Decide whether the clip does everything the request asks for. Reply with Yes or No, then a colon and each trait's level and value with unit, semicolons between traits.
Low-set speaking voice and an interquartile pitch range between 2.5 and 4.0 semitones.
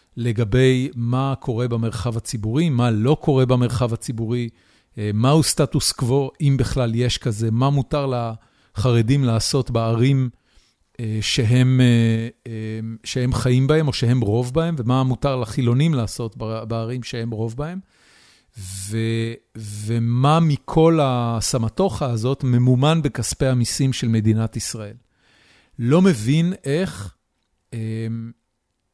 Yes: low, 120 Hz; average, 2.9 semitones